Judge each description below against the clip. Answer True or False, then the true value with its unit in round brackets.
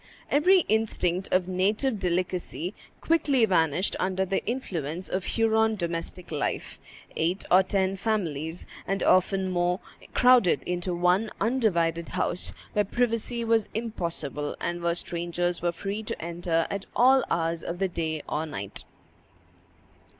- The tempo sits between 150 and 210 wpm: False (135 wpm)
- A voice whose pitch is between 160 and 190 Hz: True (185 Hz)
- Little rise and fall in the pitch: False (4.3 semitones)